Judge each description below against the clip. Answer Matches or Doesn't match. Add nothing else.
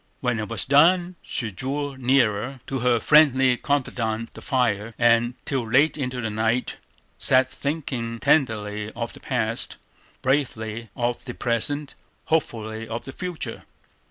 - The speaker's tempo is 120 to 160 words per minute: Matches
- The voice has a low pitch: Matches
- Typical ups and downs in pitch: Matches